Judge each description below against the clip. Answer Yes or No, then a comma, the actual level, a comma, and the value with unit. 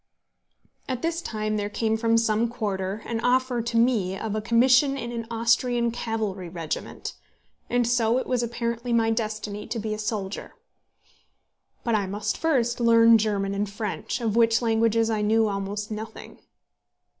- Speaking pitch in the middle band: No, high, 225 Hz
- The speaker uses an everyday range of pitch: No, narrow, 1.9 semitones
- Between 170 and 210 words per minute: No, average, 160 wpm